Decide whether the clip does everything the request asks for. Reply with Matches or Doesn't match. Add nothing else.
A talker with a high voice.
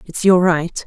Doesn't match